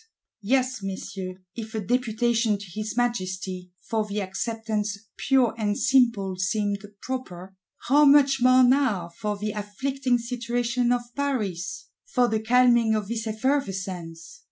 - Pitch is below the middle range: No, high, 220 Hz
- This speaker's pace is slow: Yes, slow, 130 wpm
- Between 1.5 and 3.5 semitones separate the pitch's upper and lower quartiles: No, average, 4.1 semitones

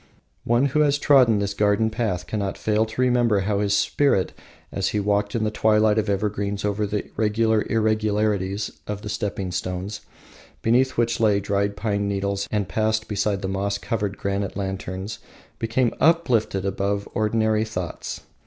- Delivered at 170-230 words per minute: No, average, 160 wpm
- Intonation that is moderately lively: No, narrow, 1.7 semitones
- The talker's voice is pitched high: No, low, 105 Hz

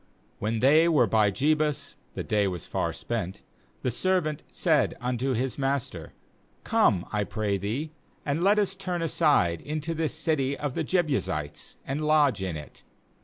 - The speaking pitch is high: No, low, 135 Hz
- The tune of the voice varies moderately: No, wide, 6.6 semitones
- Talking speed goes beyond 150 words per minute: Yes, average, 165 wpm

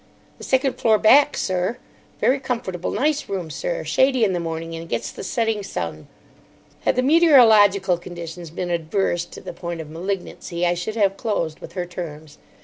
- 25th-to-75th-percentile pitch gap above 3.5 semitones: Yes, average, 5.3 semitones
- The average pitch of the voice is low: No, medium, 185 Hz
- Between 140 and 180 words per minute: Yes, average, 175 wpm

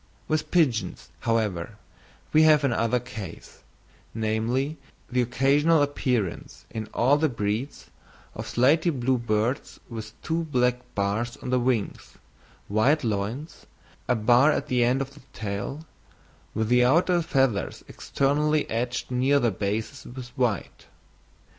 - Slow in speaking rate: Yes, slow, 130 wpm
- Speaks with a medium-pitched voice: No, low, 125 Hz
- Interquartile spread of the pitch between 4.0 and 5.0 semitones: Yes, average, 4.3 semitones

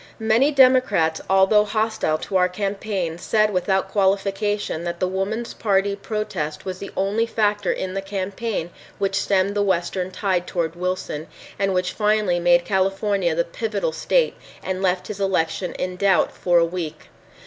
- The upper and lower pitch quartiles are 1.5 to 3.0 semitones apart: Yes, narrow, 2.4 semitones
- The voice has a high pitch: Yes, high, 195 Hz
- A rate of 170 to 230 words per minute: No, average, 160 wpm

